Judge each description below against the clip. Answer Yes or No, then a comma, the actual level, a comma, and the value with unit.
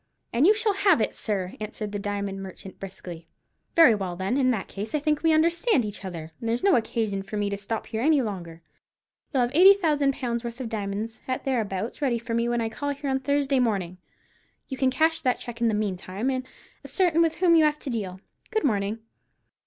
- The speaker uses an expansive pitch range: Yes, wide, 6.0 semitones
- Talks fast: Yes, fast, 220 wpm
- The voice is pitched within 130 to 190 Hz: No, high, 235 Hz